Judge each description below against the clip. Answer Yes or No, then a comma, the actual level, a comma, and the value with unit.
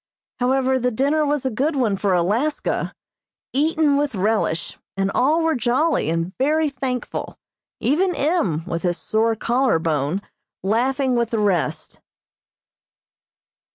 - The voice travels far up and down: Yes, wide, 6.3 semitones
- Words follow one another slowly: Yes, slow, 130 wpm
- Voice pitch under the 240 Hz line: No, very high, 250 Hz